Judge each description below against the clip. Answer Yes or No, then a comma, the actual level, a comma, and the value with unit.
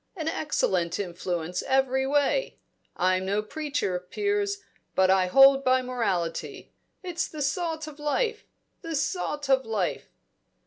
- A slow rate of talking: Yes, slow, 130 wpm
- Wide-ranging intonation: Yes, wide, 8.8 semitones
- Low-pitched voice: No, very high, 270 Hz